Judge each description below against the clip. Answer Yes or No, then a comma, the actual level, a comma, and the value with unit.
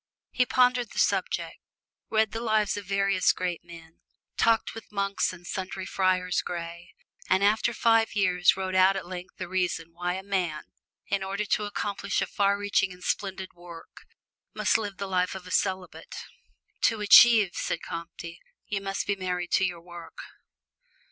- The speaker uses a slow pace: No, average, 170 wpm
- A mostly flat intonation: Yes, narrow, 2.3 semitones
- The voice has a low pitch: No, high, 190 Hz